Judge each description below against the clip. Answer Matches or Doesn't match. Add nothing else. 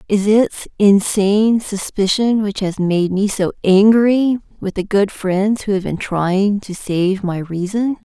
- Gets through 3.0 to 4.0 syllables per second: Matches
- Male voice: Doesn't match